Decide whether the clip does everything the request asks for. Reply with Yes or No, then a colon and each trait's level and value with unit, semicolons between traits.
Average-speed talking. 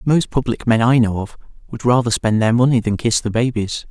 No: fast, 230 wpm